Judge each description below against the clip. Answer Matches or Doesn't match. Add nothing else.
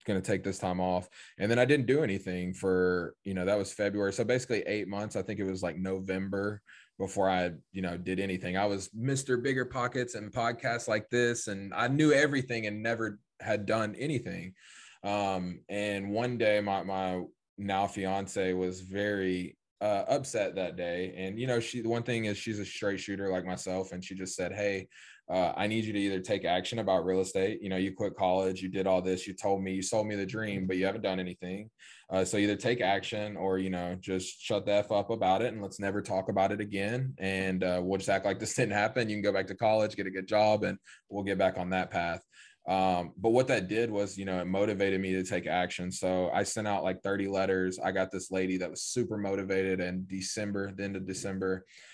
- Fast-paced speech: Matches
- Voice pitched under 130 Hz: Matches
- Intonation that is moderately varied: Doesn't match